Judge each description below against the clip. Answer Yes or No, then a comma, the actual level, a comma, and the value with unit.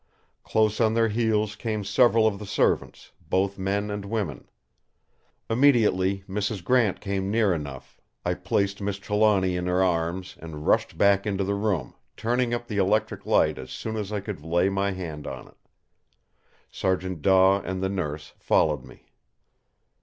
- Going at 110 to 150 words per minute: No, average, 160 wpm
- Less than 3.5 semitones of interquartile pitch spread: Yes, narrow, 2.6 semitones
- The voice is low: Yes, low, 100 Hz